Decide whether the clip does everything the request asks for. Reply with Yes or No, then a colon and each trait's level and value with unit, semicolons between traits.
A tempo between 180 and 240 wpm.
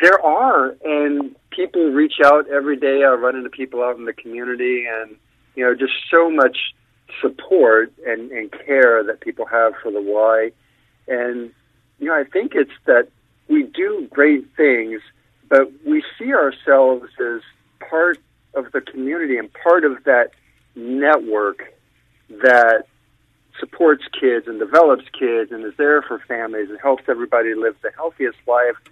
No: average, 155 wpm